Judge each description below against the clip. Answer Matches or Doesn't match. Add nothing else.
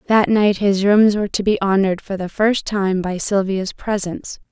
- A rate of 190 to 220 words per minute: Matches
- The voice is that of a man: Doesn't match